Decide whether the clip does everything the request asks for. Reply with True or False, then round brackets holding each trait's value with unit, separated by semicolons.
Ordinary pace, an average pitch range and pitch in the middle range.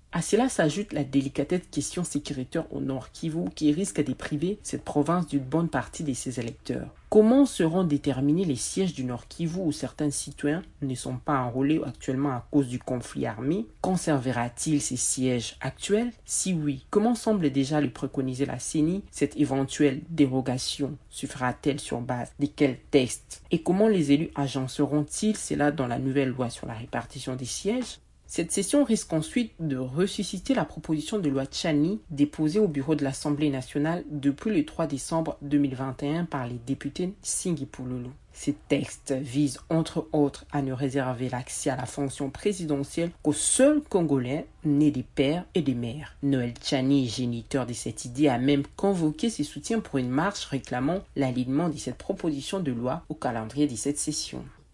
True (170 wpm; 3.6 semitones; 145 Hz)